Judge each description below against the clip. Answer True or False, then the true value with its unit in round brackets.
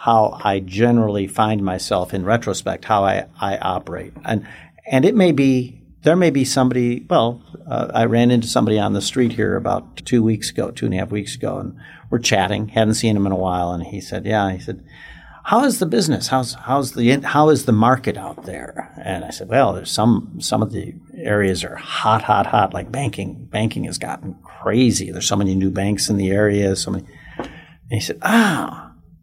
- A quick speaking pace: True (210 wpm)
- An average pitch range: True (4.1 semitones)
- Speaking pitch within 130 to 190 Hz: False (110 Hz)